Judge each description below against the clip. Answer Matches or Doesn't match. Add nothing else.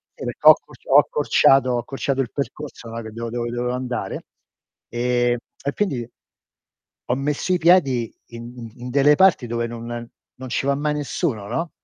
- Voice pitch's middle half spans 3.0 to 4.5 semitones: Matches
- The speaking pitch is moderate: Doesn't match